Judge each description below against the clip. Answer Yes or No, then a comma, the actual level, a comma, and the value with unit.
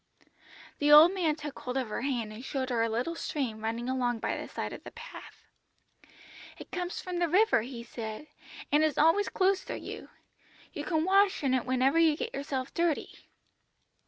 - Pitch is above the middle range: Yes, very high, 285 Hz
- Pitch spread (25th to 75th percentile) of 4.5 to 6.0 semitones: Yes, wide, 5.4 semitones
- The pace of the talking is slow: No, average, 190 wpm